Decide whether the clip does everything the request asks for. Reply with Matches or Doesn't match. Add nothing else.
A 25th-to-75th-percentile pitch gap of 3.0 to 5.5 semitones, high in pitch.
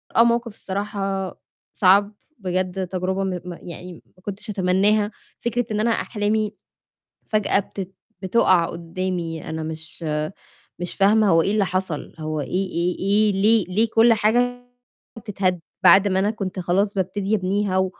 Doesn't match